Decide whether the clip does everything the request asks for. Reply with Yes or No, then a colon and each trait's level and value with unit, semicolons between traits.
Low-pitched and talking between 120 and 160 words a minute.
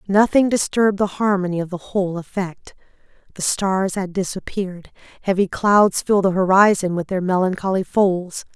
No: high, 190 Hz; average, 145 wpm